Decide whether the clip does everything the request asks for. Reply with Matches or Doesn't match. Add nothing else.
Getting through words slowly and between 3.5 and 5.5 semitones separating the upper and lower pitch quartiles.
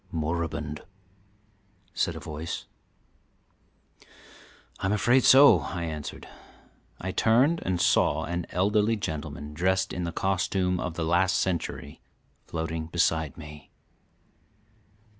Doesn't match